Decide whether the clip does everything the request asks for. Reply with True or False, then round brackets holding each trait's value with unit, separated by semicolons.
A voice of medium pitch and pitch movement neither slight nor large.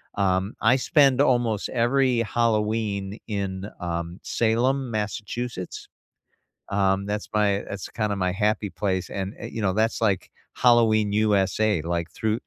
False (105 Hz; 3.1 semitones)